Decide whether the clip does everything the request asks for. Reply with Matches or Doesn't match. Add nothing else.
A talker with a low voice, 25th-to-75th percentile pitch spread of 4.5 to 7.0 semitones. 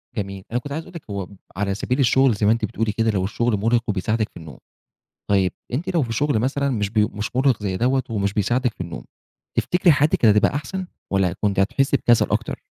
Matches